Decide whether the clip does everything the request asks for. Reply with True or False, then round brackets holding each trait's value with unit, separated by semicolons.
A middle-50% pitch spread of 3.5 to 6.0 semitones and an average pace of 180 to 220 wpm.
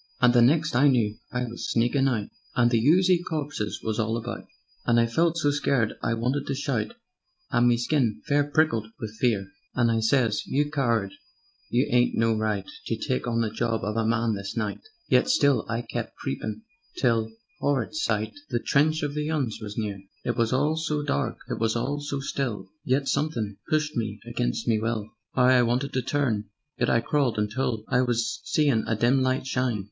True (4.0 semitones; 200 wpm)